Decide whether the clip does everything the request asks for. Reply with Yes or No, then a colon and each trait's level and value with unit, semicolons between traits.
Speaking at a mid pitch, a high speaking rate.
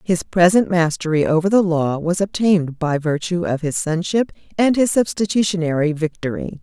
No: medium, 175 Hz; average, 155 wpm